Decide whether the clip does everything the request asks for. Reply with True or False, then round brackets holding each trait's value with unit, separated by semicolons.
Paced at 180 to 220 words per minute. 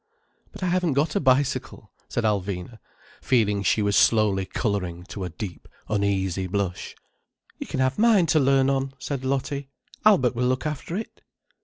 False (165 wpm)